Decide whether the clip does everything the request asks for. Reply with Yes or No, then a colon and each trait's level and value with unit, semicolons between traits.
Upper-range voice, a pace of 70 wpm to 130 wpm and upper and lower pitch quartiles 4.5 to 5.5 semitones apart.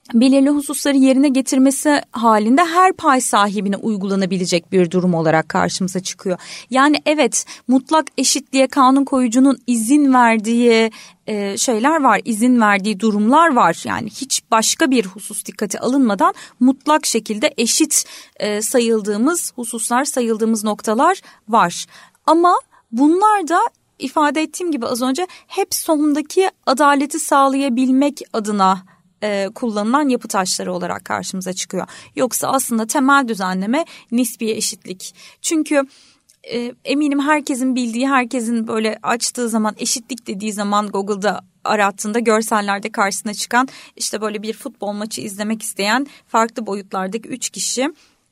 Yes: high, 240 Hz; average, 120 wpm; average, 4.9 semitones